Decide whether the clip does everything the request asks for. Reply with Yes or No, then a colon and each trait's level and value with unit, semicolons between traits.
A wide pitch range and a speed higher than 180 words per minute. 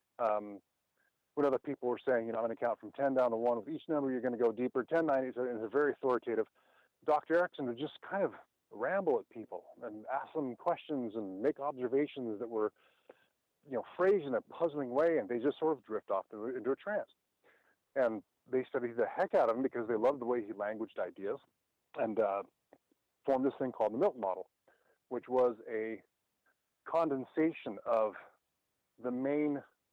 No: average, 3.8 semitones; average, 200 wpm